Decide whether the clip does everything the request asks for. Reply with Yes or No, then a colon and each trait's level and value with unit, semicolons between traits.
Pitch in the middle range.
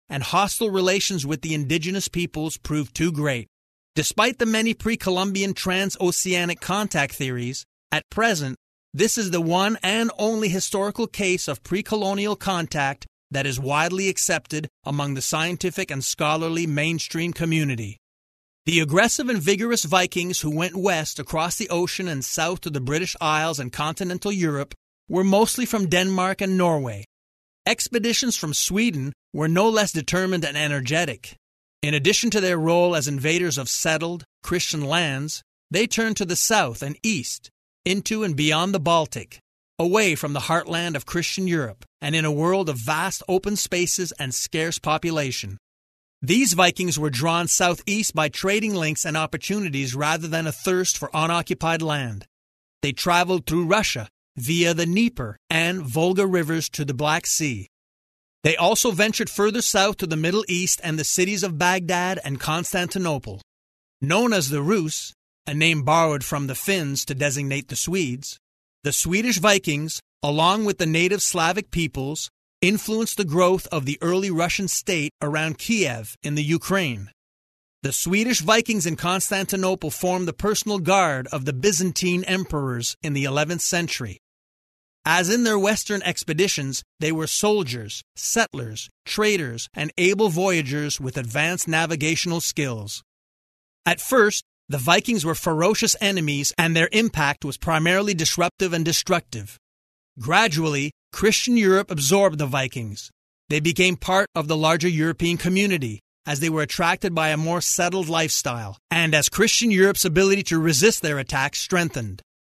Yes: medium, 165 Hz